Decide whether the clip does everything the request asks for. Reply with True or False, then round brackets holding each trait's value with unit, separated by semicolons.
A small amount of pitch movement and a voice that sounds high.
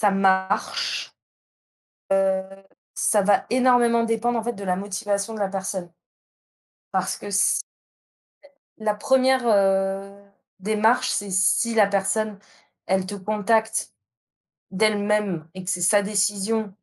True (2.3 semitones; 205 Hz)